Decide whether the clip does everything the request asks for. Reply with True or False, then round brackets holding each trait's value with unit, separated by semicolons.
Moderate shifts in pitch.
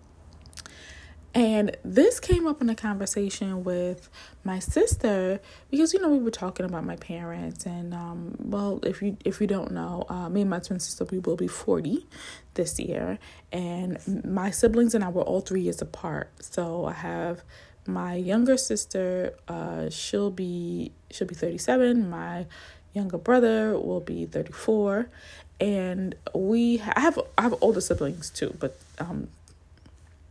True (3.9 semitones)